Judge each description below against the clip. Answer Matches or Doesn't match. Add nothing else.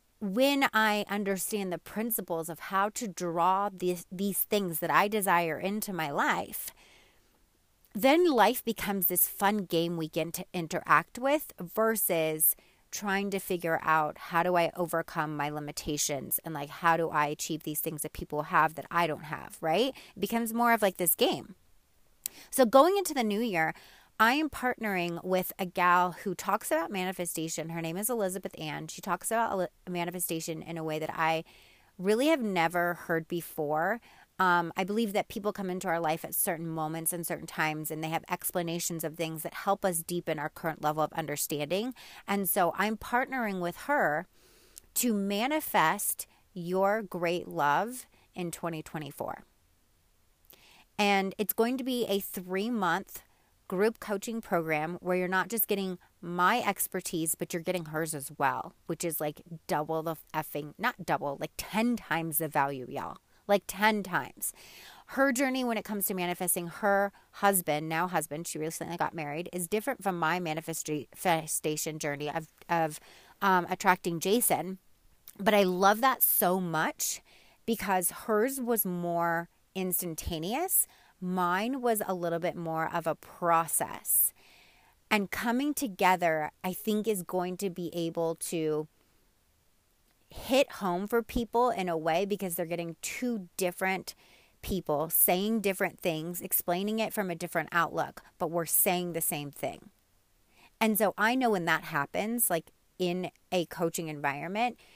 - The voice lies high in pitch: Doesn't match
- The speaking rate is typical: Matches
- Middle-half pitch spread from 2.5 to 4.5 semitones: Matches